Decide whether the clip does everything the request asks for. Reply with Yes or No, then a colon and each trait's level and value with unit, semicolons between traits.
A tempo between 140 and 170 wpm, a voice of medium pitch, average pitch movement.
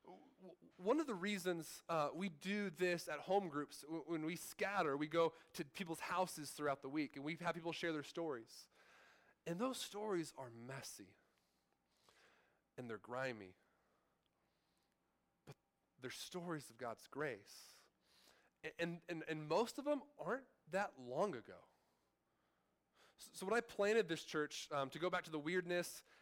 Yes: average, 155 wpm; medium, 170 Hz; average, 4.3 semitones